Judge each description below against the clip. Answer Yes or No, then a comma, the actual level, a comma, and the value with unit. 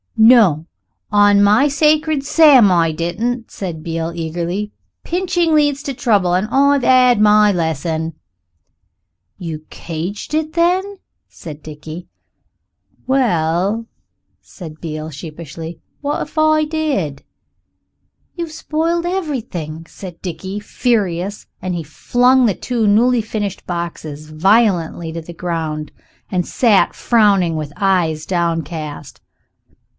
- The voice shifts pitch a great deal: Yes, wide, 7.6 semitones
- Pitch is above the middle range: Yes, high, 195 Hz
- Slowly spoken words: Yes, slow, 110 wpm